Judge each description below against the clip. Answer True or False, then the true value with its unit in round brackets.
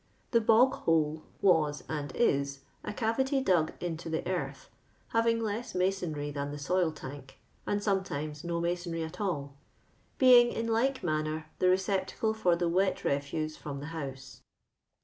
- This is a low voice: False (170 Hz)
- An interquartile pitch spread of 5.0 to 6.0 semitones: True (5.6 semitones)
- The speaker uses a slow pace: False (155 wpm)